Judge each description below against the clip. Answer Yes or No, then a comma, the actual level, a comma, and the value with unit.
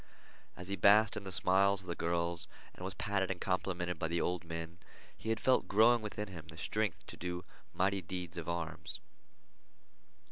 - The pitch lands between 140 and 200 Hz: No, very low, 90 Hz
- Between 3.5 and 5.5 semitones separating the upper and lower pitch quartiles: No, narrow, 2.6 semitones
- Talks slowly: No, average, 185 wpm